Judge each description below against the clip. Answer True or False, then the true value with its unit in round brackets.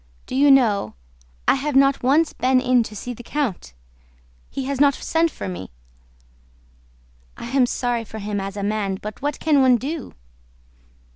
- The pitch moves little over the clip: False (4.6 semitones)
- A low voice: False (250 Hz)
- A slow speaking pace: False (170 wpm)